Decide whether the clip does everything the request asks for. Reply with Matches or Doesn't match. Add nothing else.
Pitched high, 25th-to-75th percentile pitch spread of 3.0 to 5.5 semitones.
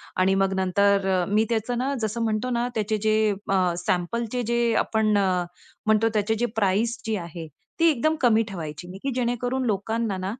Matches